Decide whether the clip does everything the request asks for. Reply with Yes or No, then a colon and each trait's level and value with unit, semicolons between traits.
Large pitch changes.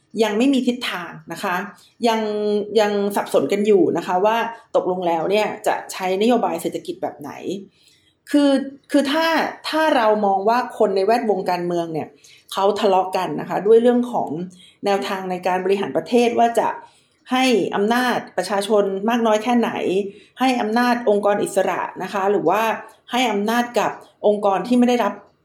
No: average, 3.5 semitones